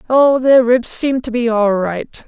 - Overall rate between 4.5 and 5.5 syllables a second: No, 3.8 syllables/s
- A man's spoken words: No, female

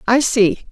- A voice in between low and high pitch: No, high, 225 Hz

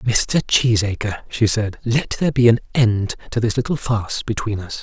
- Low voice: Yes, low, 110 Hz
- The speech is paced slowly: No, average, 185 wpm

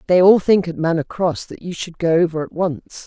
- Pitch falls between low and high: Yes, medium, 170 Hz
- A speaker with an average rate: No, fast, 255 wpm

